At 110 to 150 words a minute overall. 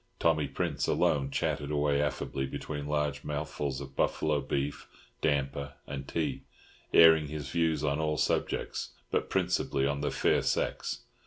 Yes: average, 145 wpm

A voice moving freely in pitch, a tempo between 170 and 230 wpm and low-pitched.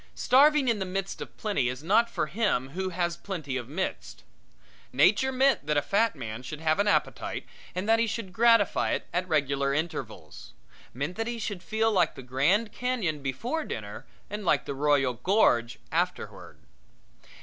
No: wide, 8.0 semitones; average, 175 wpm; medium, 185 Hz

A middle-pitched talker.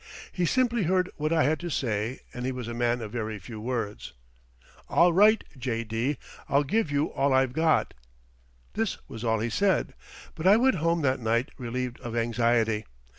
No: low, 130 Hz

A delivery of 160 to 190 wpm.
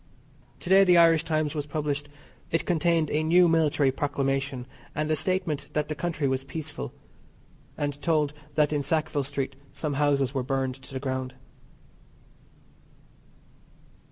No: average, 145 wpm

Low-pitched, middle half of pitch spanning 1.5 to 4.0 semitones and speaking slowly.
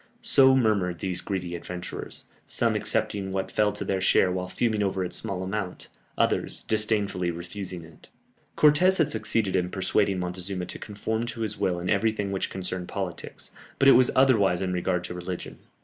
No: very low, 95 Hz; average, 3.1 semitones; average, 175 wpm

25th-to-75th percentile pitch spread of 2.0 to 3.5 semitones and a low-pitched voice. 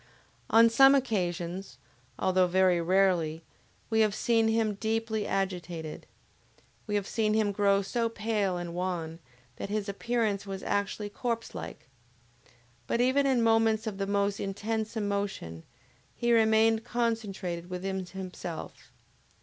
No: average, 3.2 semitones; high, 205 Hz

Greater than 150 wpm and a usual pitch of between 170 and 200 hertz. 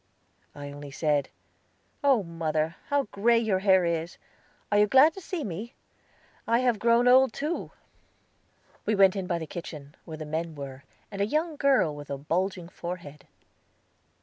Yes: average, 165 wpm; medium, 185 Hz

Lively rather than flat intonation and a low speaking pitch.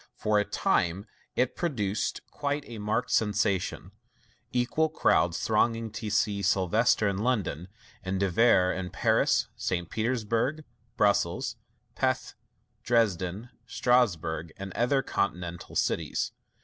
No: average, 4.2 semitones; low, 105 Hz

